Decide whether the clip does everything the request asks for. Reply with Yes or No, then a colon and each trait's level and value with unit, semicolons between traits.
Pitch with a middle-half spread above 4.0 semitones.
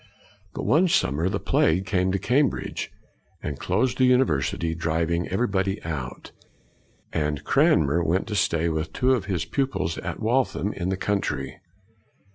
Yes: average, 5.1 semitones